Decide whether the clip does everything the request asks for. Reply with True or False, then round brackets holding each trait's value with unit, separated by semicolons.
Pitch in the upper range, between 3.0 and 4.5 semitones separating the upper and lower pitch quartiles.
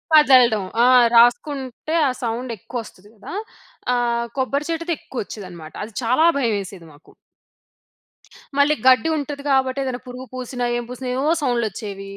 True (250 Hz; 3.5 semitones)